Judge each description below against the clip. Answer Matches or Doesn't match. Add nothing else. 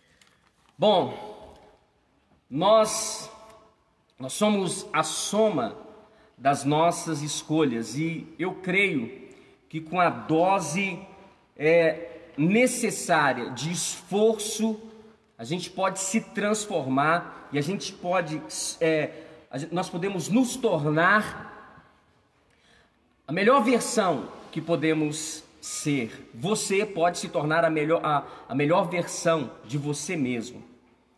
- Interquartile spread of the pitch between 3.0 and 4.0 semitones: Doesn't match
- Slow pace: Matches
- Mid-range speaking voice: Matches